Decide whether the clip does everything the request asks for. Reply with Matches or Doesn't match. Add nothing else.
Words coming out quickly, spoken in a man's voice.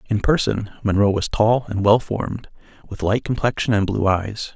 Doesn't match